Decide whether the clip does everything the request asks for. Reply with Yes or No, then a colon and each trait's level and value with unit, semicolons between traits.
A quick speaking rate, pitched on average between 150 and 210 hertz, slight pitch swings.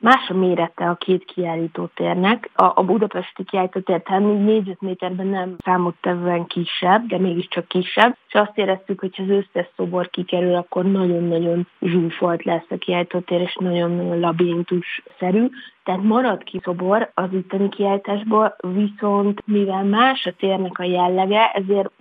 No: average, 140 wpm; medium, 185 Hz; narrow, 2.1 semitones